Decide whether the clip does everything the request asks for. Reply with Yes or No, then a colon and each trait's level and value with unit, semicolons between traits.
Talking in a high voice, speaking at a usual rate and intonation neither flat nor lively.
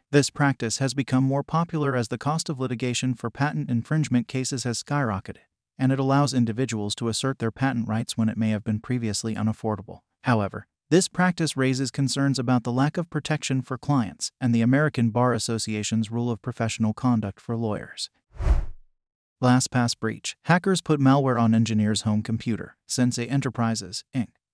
No: low, 125 Hz; average, 165 wpm; average, 3.4 semitones